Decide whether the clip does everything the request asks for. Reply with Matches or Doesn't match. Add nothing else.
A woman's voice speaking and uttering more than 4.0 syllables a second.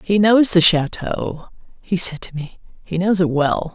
Matches